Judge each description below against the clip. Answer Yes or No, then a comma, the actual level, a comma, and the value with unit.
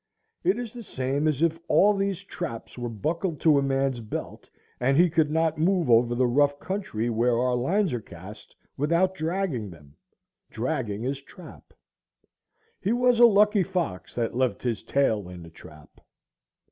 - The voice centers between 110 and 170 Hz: Yes, medium, 140 Hz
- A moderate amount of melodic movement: No, wide, 7.3 semitones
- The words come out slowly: No, average, 165 wpm